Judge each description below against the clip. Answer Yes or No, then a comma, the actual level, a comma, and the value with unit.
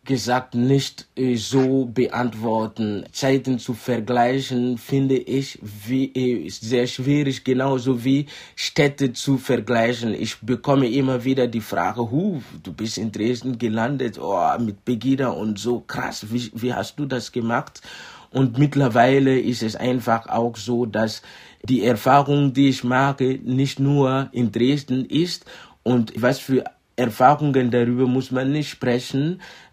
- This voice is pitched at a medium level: No, low, 125 Hz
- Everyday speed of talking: Yes, average, 135 wpm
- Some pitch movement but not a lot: No, narrow, 2.2 semitones